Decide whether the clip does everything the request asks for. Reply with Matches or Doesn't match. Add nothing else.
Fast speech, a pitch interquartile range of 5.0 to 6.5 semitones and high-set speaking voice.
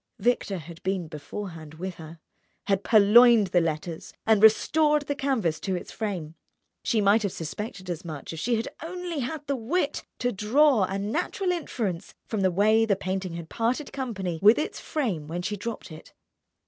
Doesn't match